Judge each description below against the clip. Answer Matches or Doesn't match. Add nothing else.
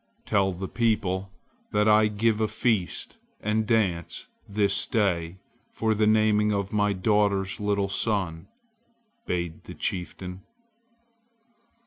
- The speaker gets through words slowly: Matches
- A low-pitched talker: Matches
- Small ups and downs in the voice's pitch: Matches